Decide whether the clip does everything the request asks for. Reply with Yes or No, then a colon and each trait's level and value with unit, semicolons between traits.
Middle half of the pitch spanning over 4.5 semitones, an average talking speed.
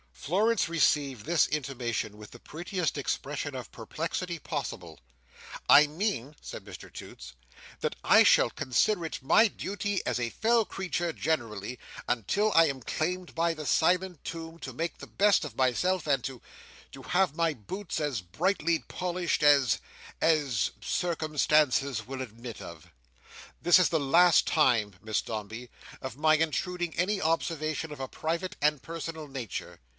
Yes: average, 5.1 semitones; average, 145 wpm